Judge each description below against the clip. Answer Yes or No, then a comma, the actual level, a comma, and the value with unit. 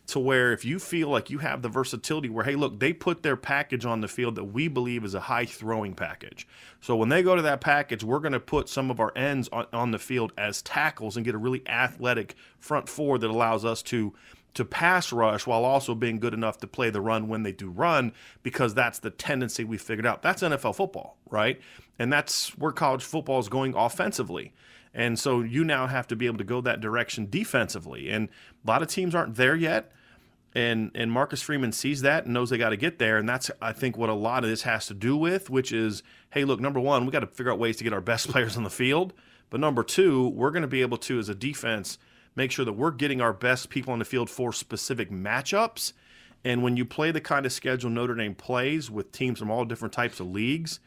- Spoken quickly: Yes, fast, 245 wpm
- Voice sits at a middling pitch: No, low, 125 Hz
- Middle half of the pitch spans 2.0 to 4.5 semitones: Yes, average, 3.3 semitones